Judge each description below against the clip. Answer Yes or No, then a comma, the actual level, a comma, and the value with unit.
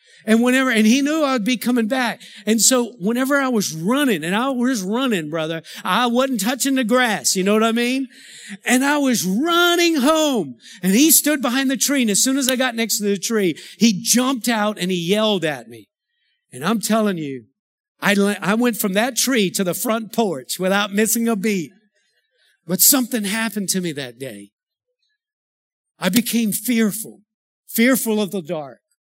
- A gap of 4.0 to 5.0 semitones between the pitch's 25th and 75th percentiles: Yes, average, 4.5 semitones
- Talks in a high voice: Yes, high, 225 Hz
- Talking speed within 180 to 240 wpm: Yes, average, 185 wpm